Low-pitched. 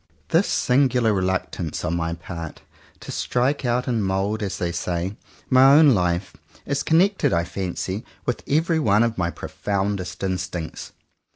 Yes: low, 100 Hz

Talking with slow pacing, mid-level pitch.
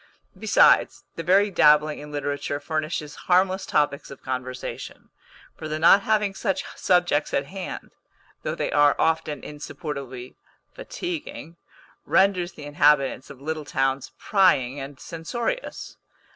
Yes: slow, 125 wpm; medium, 155 Hz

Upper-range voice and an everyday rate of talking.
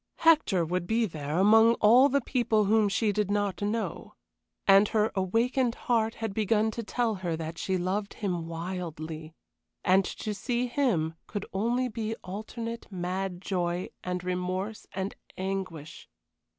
Yes: high, 200 Hz; average, 150 wpm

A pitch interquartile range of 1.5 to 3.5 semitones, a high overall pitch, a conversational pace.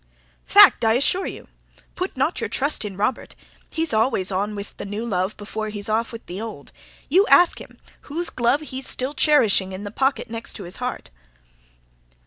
No: average, 5.2 semitones; high, 225 Hz; average, 180 wpm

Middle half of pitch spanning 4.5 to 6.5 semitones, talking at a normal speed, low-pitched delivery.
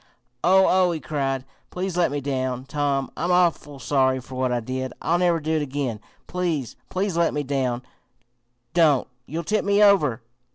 No: average, 5.0 semitones; average, 175 wpm; medium, 145 Hz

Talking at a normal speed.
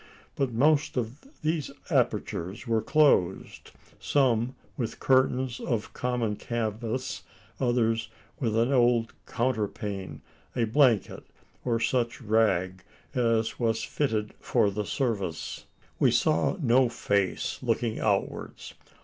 No: slow, 110 wpm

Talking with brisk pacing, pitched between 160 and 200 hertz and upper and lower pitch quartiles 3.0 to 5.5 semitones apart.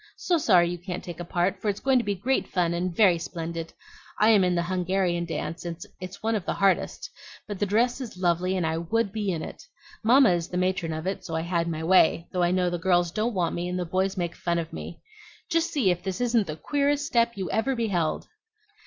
Yes: fast, 245 wpm; medium, 185 Hz; average, 3.7 semitones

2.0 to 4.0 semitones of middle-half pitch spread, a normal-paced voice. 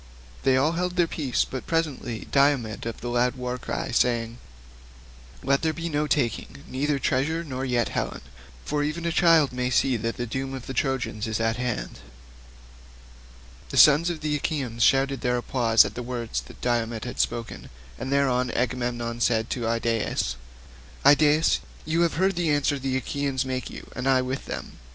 Yes: average, 3.5 semitones; average, 180 wpm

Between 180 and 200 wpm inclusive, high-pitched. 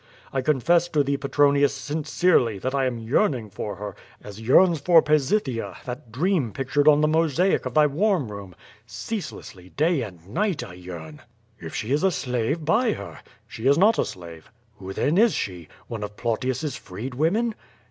No: average, 190 wpm; low, 135 Hz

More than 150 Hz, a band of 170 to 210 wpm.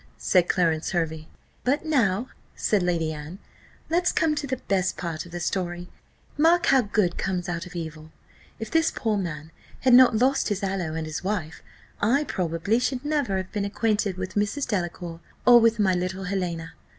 Yes: high, 190 Hz; average, 180 wpm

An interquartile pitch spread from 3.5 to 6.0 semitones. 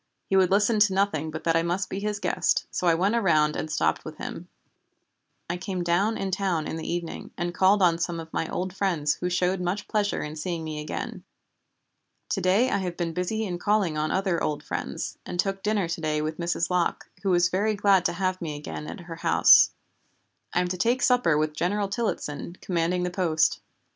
No: average, 2.9 semitones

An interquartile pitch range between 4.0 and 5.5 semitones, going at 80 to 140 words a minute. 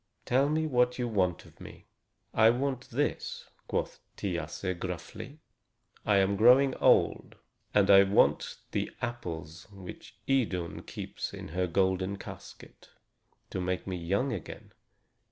Yes: average, 5.2 semitones; slow, 135 wpm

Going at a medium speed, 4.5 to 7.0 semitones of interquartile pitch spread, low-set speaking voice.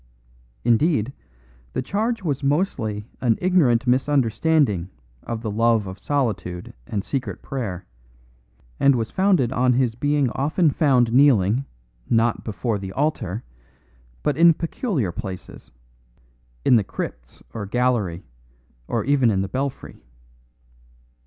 No: slow, 120 wpm; average, 5.2 semitones; low, 125 Hz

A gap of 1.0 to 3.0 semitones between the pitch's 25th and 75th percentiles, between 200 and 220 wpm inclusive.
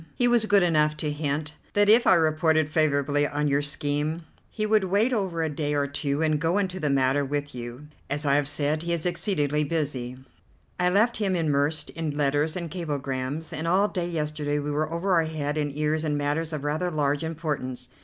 Yes: narrow, 2.6 semitones; fast, 205 wpm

